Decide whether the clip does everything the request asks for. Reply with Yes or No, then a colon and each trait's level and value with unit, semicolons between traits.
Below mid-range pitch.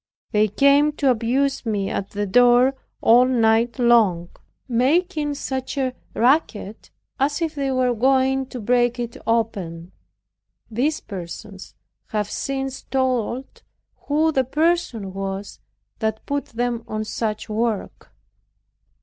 No: high, 245 Hz